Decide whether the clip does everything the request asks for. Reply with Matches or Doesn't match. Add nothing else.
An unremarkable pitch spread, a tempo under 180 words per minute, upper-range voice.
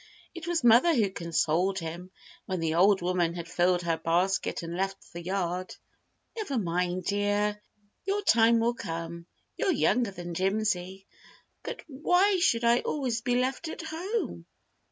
Doesn't match